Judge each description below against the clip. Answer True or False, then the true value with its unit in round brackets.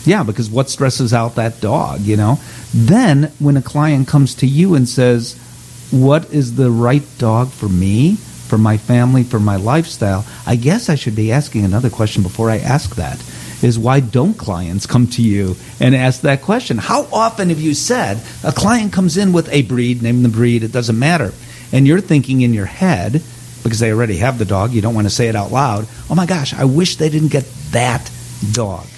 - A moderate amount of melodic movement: True (4.1 semitones)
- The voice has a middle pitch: False (125 Hz)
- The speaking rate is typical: False (210 wpm)